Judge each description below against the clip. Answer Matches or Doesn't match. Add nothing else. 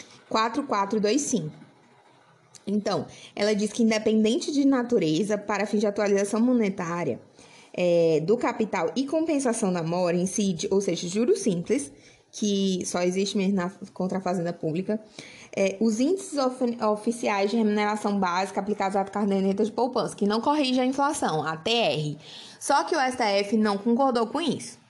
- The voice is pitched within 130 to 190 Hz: Doesn't match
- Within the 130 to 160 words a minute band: Matches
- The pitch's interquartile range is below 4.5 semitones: Matches